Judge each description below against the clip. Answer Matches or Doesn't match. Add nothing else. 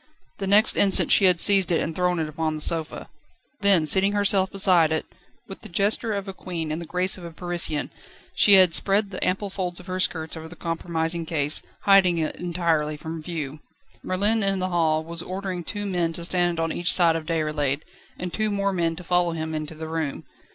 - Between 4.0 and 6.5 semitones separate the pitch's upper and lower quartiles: Doesn't match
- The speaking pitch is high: Doesn't match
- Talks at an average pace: Doesn't match